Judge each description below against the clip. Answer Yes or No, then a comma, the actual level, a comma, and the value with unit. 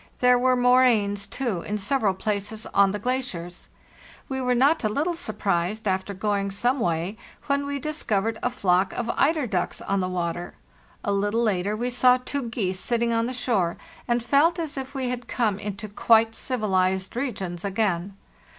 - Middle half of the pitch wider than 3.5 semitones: Yes, average, 4.3 semitones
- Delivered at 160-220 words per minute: Yes, average, 175 wpm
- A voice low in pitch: No, high, 220 Hz